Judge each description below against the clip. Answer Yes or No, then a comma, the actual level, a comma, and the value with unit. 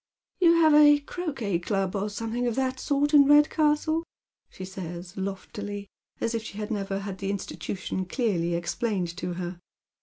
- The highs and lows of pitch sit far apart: Yes, wide, 7.0 semitones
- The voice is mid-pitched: No, high, 205 Hz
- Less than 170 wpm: No, average, 175 wpm